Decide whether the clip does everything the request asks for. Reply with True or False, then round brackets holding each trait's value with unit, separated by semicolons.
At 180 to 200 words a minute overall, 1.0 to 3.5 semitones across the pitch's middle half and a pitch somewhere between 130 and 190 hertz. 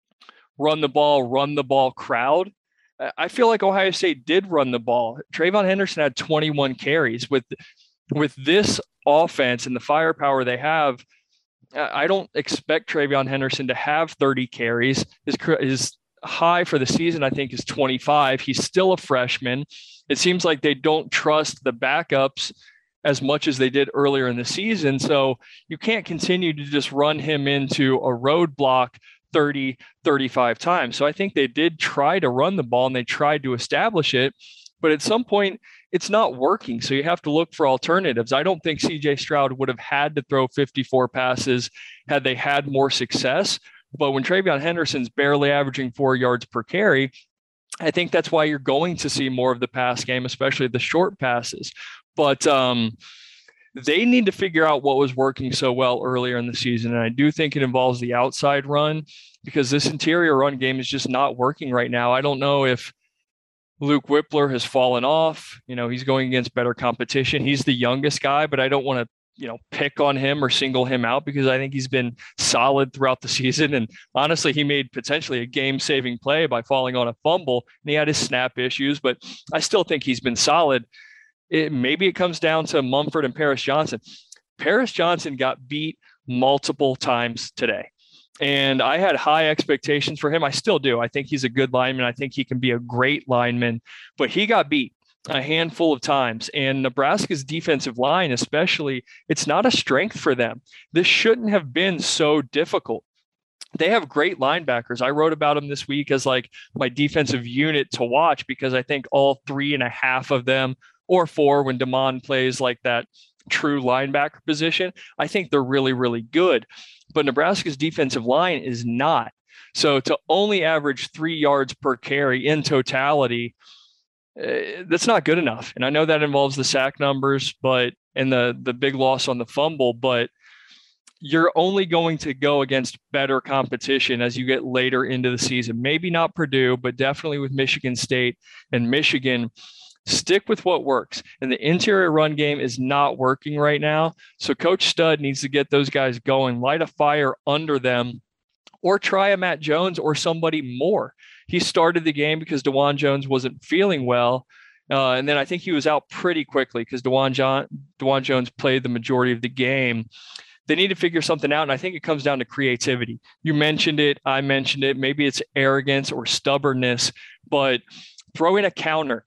True (190 wpm; 3.1 semitones; 140 Hz)